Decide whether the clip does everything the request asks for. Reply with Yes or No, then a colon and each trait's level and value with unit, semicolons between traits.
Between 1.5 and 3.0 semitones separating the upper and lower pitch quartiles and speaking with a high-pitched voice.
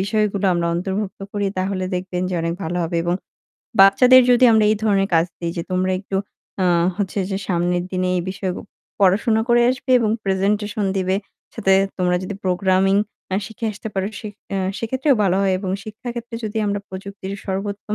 Yes: narrow, 2.4 semitones; high, 195 Hz